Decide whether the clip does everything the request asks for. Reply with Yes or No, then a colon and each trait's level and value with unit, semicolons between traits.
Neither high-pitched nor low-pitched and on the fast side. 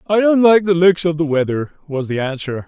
Yes: medium, 165 Hz; fast, 245 wpm